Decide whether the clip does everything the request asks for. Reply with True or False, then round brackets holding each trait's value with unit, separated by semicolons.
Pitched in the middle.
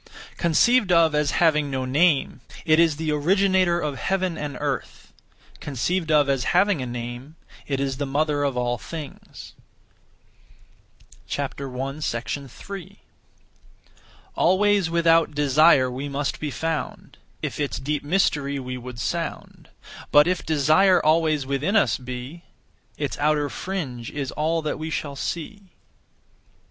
True (150 Hz)